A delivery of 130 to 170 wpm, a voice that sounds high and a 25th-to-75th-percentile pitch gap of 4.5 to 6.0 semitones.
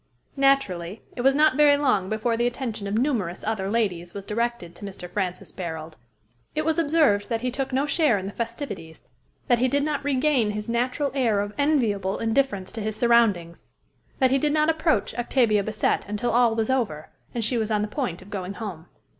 No: average, 200 wpm; high, 230 Hz; average, 5.0 semitones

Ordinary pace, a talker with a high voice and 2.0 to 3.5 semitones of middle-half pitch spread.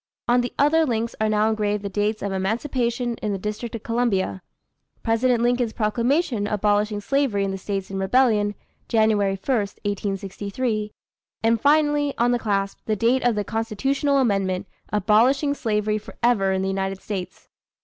Yes: average, 160 wpm; high, 215 Hz; average, 3.2 semitones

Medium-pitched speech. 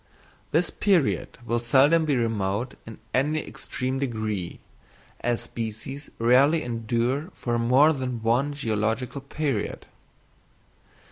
No: low, 125 Hz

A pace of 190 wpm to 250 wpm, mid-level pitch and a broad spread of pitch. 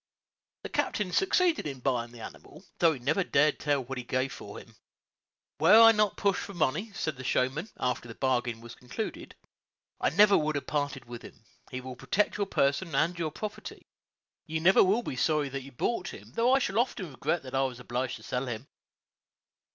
Yes: fast, 205 wpm; medium, 145 Hz; wide, 6.8 semitones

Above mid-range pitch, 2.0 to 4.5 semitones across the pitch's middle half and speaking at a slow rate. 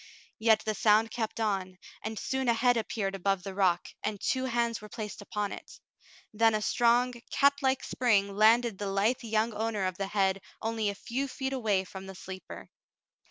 No: high, 215 Hz; average, 3.1 semitones; average, 185 wpm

